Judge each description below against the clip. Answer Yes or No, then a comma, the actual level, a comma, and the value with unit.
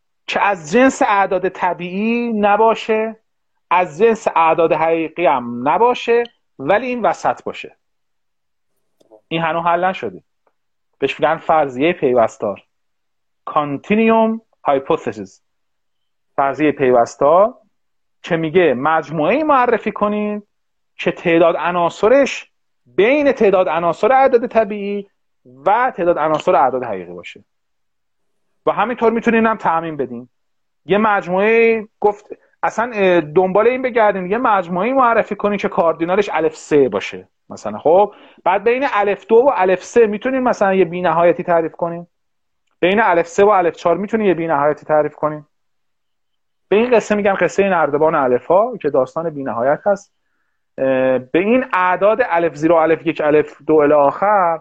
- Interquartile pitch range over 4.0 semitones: Yes, average, 5.3 semitones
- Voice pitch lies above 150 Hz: Yes, medium, 185 Hz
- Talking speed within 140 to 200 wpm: No, average, 130 wpm